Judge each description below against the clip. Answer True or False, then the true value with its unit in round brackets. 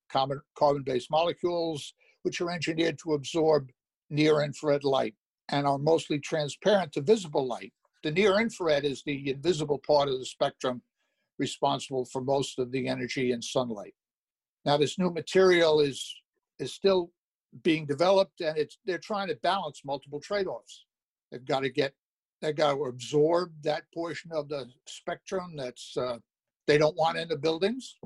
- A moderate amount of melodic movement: True (3.6 semitones)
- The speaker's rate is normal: True (150 wpm)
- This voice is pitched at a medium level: True (150 Hz)